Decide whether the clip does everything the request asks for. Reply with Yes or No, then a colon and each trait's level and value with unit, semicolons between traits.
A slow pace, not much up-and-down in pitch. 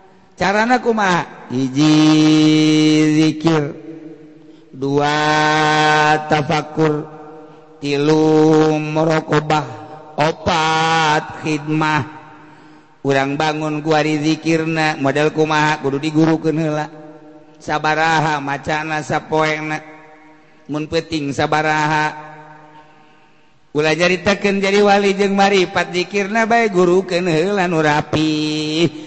Yes: slow, 70 wpm; narrow, 0.6 semitones